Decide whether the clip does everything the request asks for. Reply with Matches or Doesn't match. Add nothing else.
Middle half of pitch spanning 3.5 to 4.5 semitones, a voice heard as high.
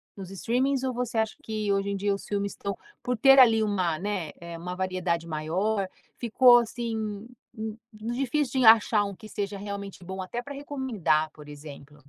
Matches